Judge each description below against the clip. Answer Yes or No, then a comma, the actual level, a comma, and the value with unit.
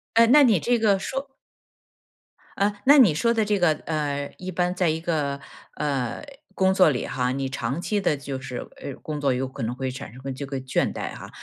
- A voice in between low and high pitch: Yes, medium, 150 Hz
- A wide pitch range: Yes, wide, 6.5 semitones